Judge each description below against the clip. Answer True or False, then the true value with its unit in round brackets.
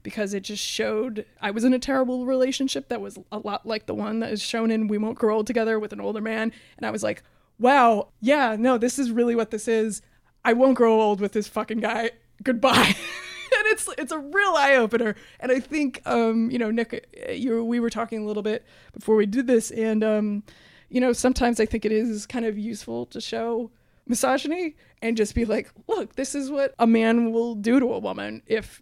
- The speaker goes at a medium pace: False (225 wpm)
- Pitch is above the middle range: True (230 Hz)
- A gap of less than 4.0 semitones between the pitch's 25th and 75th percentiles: True (2.8 semitones)